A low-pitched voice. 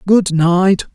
No: medium, 185 Hz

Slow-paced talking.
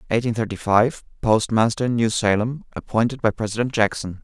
Yes: slow, 130 wpm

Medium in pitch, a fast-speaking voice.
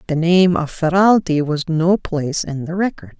No: medium, 170 Hz; average, 190 wpm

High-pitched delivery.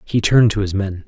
No: low, 105 Hz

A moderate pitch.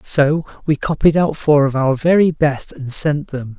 Yes: medium, 145 Hz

